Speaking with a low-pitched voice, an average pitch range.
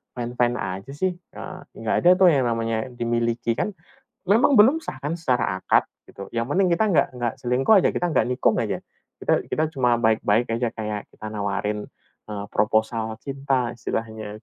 Yes: low, 120 Hz; average, 3.9 semitones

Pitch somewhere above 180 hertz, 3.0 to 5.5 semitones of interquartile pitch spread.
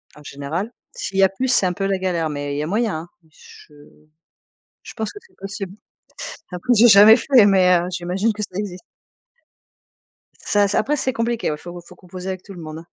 Yes: high, 190 Hz; average, 3.5 semitones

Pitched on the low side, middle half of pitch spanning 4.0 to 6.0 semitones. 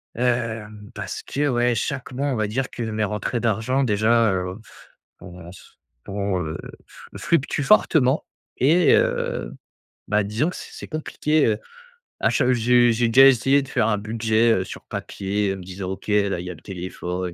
Yes: low, 110 Hz; average, 4.3 semitones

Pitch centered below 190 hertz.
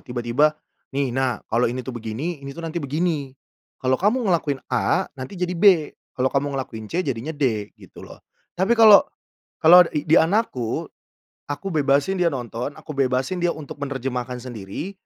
Yes: medium, 140 Hz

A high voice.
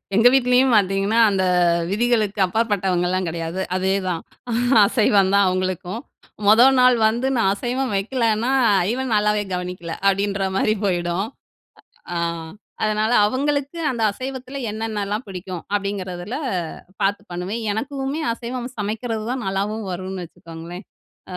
Yes: high, 205 Hz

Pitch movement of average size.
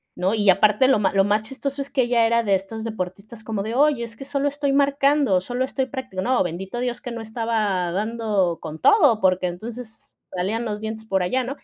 Yes: average, 4.7 semitones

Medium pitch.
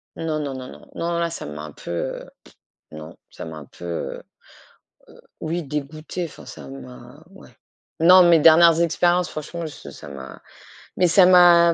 Yes: medium, 155 Hz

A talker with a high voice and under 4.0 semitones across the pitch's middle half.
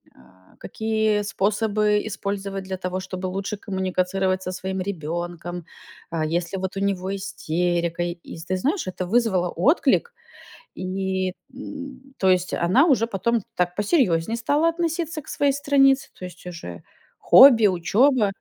No: high, 195 Hz; average, 4.3 semitones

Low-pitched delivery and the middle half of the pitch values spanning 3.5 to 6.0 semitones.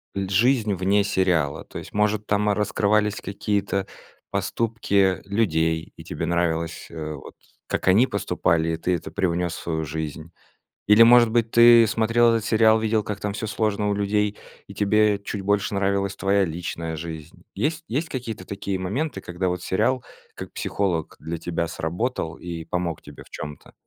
Yes: low, 100 Hz; average, 4.1 semitones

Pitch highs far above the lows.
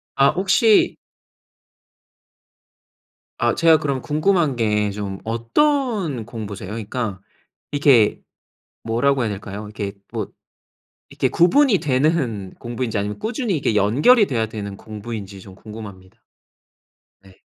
Yes: wide, 6.9 semitones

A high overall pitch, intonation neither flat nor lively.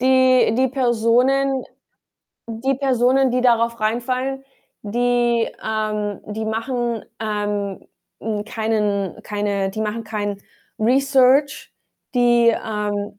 Yes: high, 230 Hz; average, 3.2 semitones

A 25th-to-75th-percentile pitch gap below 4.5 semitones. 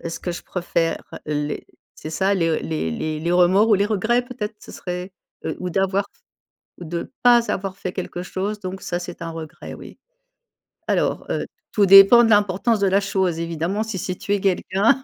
Yes: average, 3.0 semitones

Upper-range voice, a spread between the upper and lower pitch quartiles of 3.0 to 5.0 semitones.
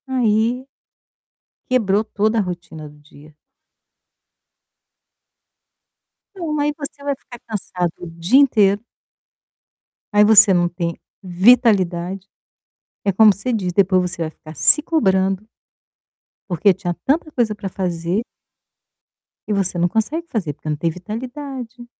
No: high, 200 Hz; wide, 5.5 semitones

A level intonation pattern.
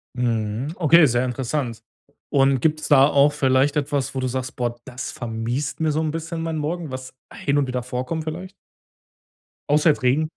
No: average, 3.5 semitones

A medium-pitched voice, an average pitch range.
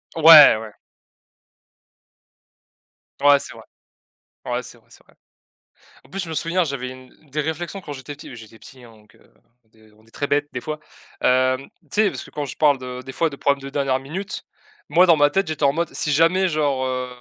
Yes: medium, 145 Hz; average, 3.7 semitones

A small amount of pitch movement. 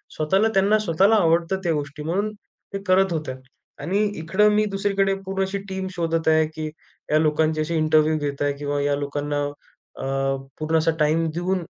No: average, 4.0 semitones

